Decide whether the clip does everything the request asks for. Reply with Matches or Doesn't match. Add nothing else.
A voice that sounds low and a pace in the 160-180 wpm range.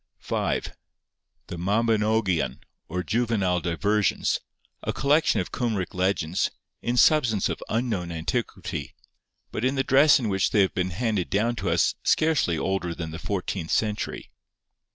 Doesn't match